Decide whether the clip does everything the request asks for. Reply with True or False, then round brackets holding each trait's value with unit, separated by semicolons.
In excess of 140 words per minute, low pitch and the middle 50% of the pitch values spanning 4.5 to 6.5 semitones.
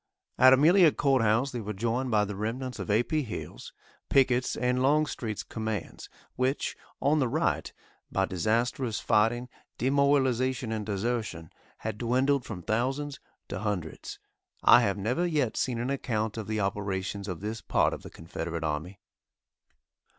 False (150 wpm; 115 Hz; 4.0 semitones)